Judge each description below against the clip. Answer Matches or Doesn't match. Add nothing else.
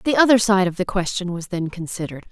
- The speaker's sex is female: Matches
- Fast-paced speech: Matches